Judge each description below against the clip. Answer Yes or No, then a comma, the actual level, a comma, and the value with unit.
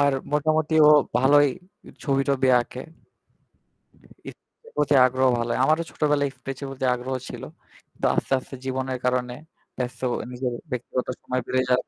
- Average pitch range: No, narrow, 2.1 semitones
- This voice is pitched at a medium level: No, low, 130 Hz